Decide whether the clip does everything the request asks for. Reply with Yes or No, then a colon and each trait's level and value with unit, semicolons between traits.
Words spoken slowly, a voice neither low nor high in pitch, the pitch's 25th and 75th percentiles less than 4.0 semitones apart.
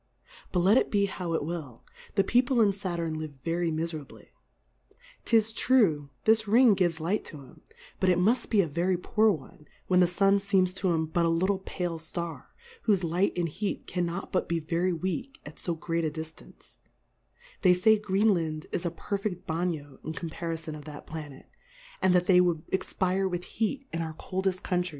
No: average, 185 wpm; medium, 180 Hz; average, 3.2 semitones